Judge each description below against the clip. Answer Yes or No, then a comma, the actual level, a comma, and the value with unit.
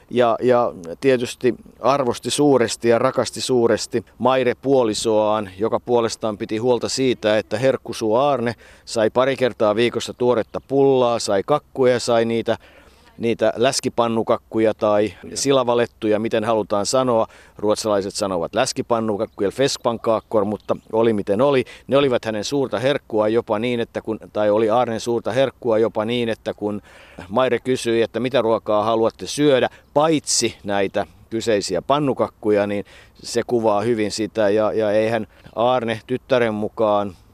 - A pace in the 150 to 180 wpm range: No, average, 135 wpm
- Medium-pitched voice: No, low, 115 Hz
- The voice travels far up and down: No, narrow, 2.5 semitones